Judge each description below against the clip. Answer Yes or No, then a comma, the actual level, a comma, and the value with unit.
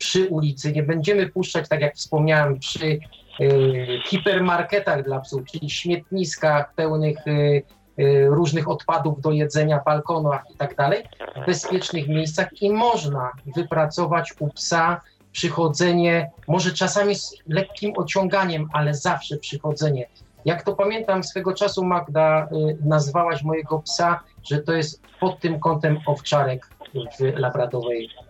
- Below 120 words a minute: No, average, 130 wpm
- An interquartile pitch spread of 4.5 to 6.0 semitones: No, average, 3.3 semitones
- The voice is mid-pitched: Yes, medium, 155 Hz